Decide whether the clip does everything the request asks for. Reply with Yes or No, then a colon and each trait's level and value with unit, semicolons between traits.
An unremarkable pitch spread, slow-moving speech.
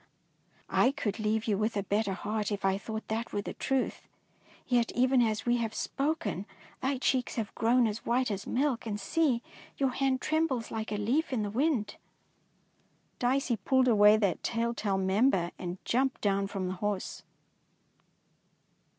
No: average, 3.8 semitones; average, 165 wpm